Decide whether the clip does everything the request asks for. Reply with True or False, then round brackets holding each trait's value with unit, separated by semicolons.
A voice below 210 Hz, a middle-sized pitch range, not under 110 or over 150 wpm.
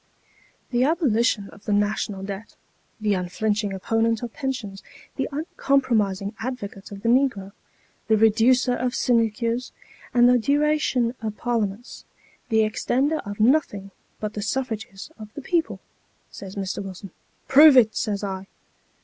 False (220 Hz; 3.8 semitones; 145 wpm)